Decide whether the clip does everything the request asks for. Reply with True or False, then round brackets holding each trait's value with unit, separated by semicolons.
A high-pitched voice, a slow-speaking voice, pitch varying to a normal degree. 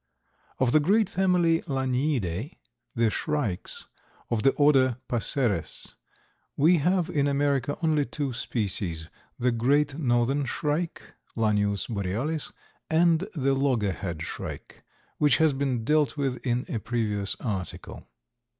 False (135 Hz; 125 wpm; 4.8 semitones)